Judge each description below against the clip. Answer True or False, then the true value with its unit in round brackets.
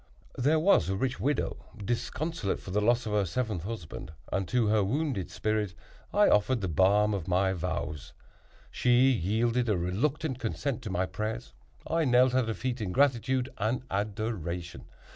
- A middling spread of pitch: True (4.9 semitones)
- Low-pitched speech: True (110 Hz)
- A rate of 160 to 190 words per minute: True (165 wpm)